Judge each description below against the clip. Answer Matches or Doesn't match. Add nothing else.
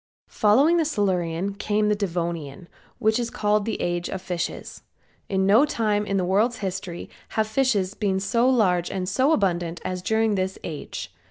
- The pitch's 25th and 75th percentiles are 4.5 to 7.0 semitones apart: Doesn't match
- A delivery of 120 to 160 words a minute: Doesn't match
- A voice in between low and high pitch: Doesn't match